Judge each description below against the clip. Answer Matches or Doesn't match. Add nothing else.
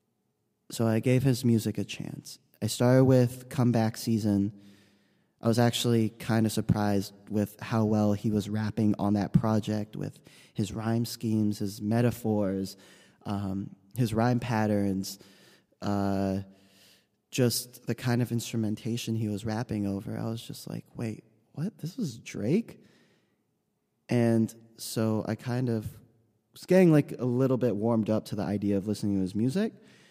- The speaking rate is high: Doesn't match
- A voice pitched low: Matches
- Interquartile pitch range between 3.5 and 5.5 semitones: Doesn't match